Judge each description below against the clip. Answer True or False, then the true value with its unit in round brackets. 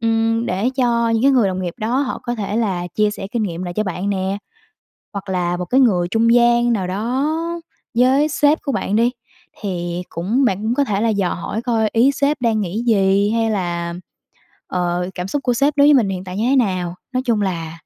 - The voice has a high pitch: True (215 Hz)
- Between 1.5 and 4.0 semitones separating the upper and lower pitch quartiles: False (4.6 semitones)